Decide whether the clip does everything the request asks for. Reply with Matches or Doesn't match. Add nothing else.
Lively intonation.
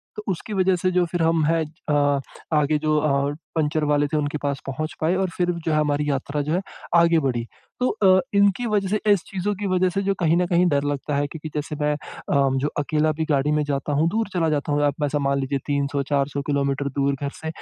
Doesn't match